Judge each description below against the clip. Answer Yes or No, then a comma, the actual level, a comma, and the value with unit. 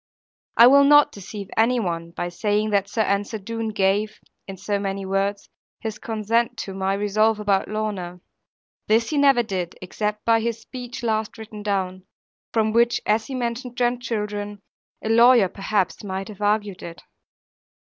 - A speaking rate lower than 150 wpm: No, average, 160 wpm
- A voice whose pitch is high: Yes, high, 210 Hz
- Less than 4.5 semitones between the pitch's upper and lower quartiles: Yes, average, 2.7 semitones